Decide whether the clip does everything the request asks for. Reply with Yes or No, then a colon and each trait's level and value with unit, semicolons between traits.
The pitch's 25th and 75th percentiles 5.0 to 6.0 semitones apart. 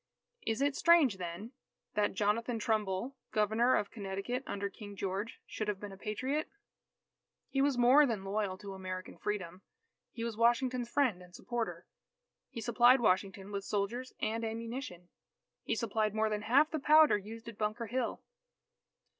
No: average, 3.5 semitones